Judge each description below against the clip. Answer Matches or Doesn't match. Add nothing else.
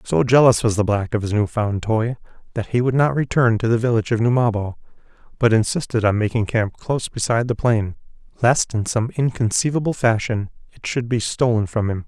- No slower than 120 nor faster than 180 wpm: Doesn't match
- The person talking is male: Matches